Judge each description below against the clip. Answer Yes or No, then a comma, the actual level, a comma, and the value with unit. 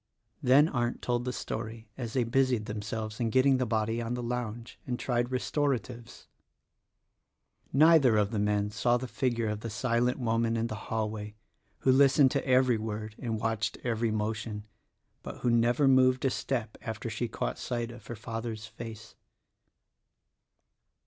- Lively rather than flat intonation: No, narrow, 2.4 semitones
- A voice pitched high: No, low, 115 Hz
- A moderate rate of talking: Yes, average, 160 wpm